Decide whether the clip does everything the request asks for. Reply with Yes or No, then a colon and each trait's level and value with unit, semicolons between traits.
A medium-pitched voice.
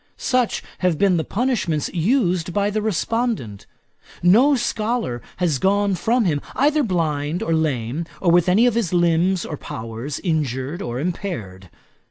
Yes: medium, 175 Hz